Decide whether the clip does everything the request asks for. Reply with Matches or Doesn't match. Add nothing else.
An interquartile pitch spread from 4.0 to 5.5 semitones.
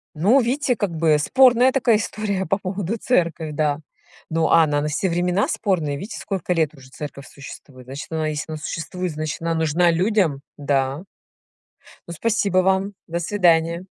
Matches